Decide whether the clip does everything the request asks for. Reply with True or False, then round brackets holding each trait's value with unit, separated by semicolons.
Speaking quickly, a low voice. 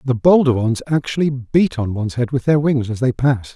True (235 wpm; 130 Hz)